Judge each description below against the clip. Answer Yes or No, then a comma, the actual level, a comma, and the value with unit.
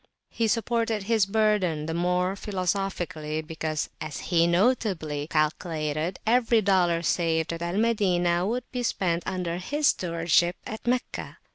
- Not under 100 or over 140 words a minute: Yes, slow, 135 wpm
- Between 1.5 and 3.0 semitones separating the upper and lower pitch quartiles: No, average, 4.4 semitones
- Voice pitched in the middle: Yes, medium, 180 Hz